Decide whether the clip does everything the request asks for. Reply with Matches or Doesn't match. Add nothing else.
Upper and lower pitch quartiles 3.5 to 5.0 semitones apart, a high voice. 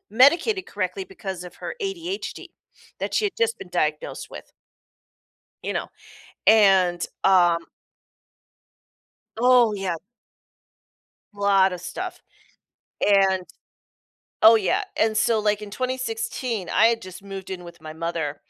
Doesn't match